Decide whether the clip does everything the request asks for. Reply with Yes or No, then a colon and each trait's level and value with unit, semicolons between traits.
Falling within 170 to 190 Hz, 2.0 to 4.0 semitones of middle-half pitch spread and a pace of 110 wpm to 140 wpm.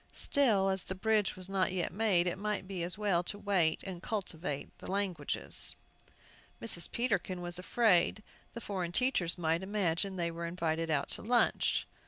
No: medium, 185 Hz; average, 3.0 semitones; average, 170 wpm